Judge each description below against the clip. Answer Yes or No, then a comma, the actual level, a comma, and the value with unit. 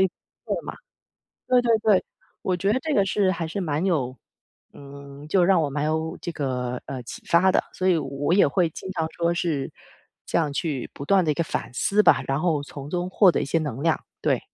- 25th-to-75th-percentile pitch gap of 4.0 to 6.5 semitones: Yes, average, 4.6 semitones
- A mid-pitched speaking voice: Yes, medium, 165 Hz